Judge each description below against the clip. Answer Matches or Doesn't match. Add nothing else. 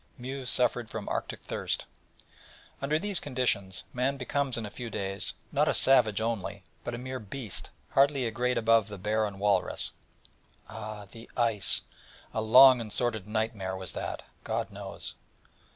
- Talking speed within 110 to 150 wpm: Doesn't match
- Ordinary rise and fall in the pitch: Matches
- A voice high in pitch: Doesn't match